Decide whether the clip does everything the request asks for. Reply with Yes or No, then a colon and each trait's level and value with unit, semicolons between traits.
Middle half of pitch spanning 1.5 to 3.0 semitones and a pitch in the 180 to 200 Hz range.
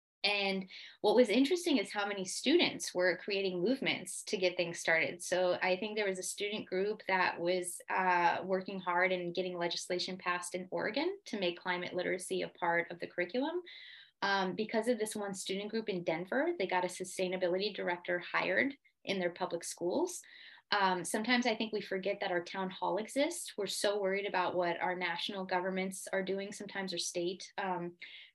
Yes: narrow, 2.6 semitones; high, 190 Hz